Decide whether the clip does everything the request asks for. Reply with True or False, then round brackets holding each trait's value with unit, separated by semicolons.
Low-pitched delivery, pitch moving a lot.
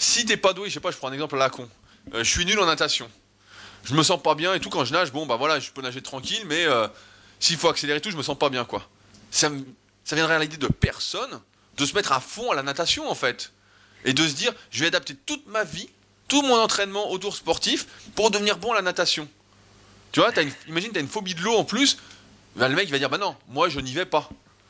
False (155 Hz; 7.6 semitones)